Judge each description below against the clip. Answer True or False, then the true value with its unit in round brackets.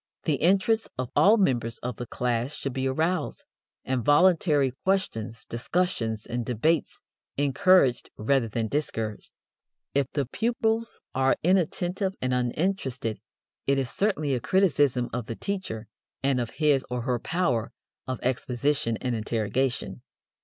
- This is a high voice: False (135 Hz)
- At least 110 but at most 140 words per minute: True (135 wpm)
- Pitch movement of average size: False (6.4 semitones)